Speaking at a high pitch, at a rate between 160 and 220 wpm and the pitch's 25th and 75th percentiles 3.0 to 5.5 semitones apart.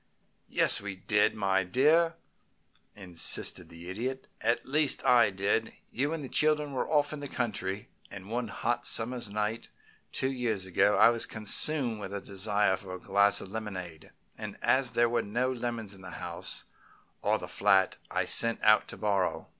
No: low, 110 Hz; average, 175 wpm; average, 4.3 semitones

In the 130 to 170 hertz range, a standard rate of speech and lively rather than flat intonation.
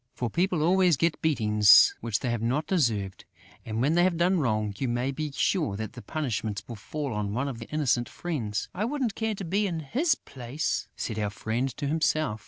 No: medium, 140 Hz; fast, 210 wpm; wide, 7.1 semitones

